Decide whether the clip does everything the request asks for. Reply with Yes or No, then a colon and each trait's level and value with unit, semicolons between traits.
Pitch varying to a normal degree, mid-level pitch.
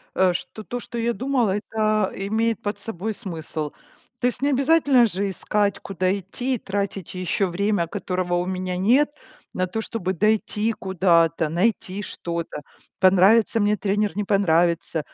No: average, 3.4 semitones; high, 200 Hz